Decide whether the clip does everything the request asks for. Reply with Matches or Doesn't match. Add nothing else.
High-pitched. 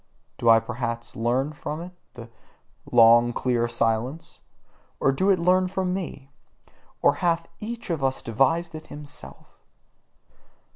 Doesn't match